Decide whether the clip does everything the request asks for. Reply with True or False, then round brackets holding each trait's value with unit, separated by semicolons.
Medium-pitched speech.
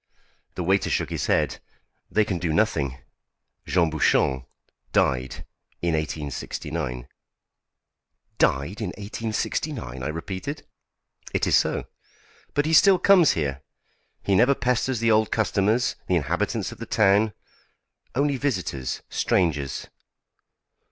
False (95 Hz)